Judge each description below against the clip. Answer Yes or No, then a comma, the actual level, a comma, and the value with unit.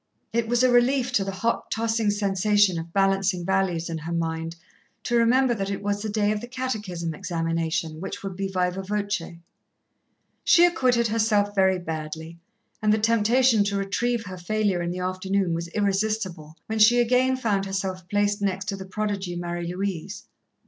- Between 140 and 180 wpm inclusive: Yes, average, 175 wpm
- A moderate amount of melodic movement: Yes, average, 3.6 semitones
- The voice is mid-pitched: No, high, 195 Hz